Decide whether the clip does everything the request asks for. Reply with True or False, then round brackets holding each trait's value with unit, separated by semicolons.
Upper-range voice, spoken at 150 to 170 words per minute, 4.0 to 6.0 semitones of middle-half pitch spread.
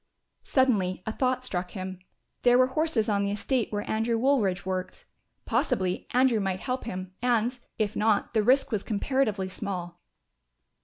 True (215 Hz; 155 wpm; 5.0 semitones)